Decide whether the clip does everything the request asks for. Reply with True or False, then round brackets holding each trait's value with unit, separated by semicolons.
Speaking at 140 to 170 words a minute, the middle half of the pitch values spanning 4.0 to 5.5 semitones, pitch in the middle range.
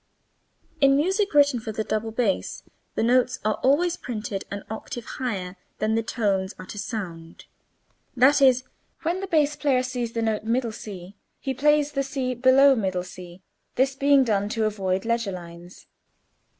False (150 wpm; 5.0 semitones; 230 Hz)